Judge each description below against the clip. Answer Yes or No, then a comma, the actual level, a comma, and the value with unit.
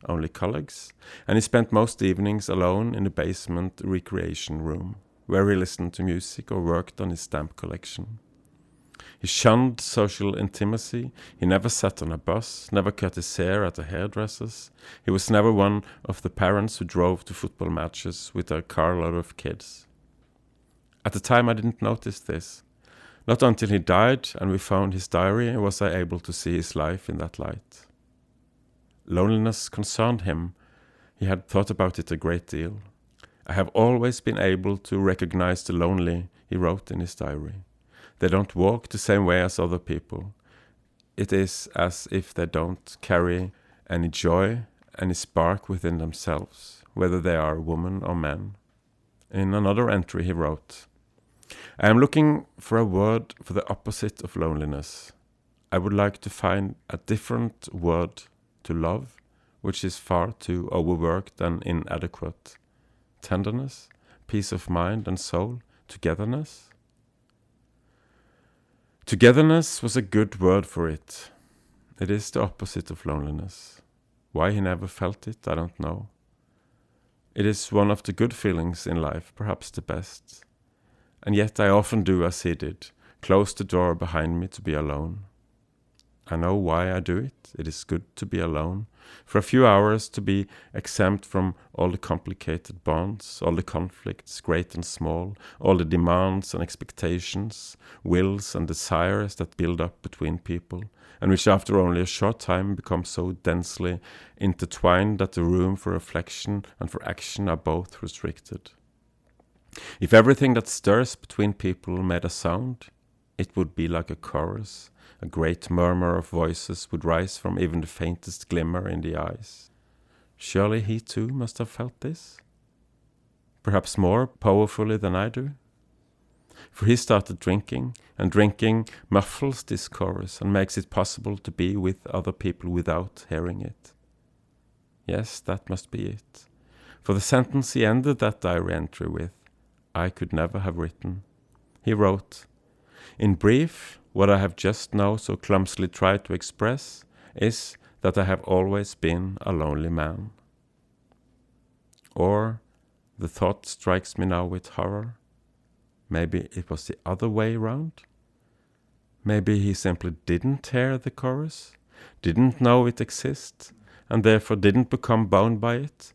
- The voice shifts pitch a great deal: No, average, 4.0 semitones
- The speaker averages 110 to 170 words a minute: Yes, average, 155 wpm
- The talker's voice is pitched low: Yes, very low, 95 Hz